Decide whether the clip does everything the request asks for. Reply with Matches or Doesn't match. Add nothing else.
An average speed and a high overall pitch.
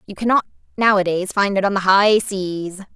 Matches